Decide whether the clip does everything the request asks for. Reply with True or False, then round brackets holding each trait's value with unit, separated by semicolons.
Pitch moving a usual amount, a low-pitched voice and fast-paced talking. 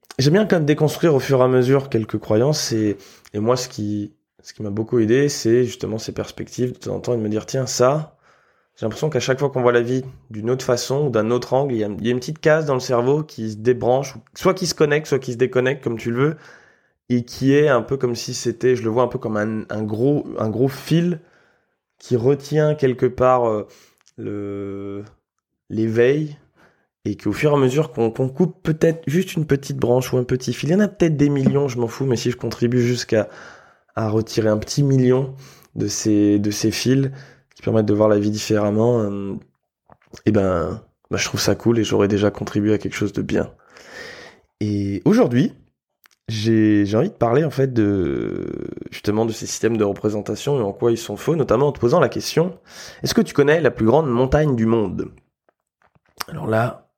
True (4.1 semitones; 120 Hz; 225 wpm)